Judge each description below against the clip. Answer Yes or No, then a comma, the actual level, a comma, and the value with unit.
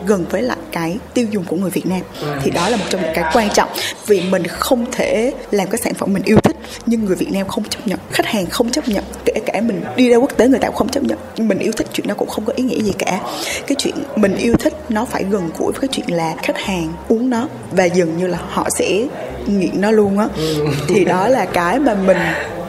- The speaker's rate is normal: No, fast, 265 wpm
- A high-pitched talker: Yes, high, 210 Hz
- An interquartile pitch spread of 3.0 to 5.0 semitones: No, wide, 5.6 semitones